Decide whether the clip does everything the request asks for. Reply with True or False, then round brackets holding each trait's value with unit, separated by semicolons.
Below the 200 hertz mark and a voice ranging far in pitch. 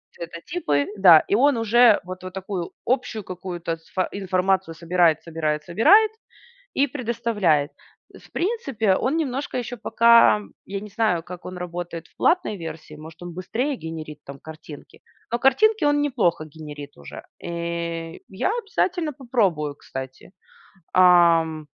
True (185 Hz; 6.4 semitones)